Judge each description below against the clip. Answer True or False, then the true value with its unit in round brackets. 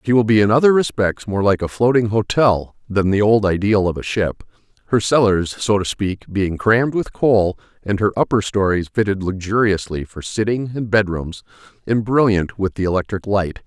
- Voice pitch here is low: True (105 Hz)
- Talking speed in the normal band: True (195 wpm)